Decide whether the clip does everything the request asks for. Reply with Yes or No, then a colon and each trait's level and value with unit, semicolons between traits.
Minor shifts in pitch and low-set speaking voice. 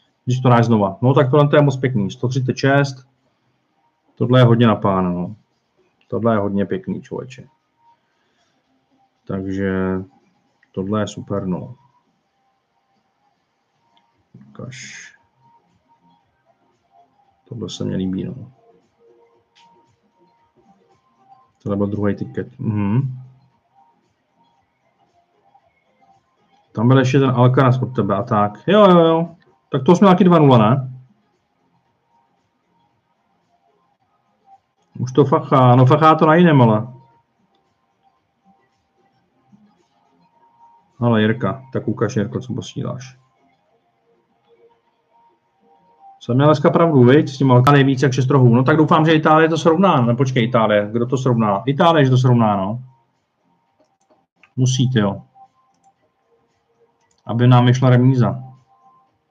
No: average, 5.2 semitones; low, 130 Hz